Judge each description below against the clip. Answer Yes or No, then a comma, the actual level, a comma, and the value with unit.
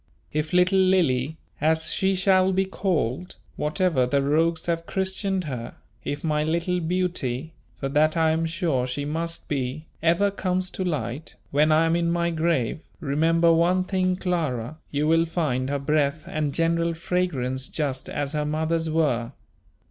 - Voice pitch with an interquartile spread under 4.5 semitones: Yes, average, 3.5 semitones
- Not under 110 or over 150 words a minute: No, average, 160 wpm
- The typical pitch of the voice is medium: Yes, medium, 160 Hz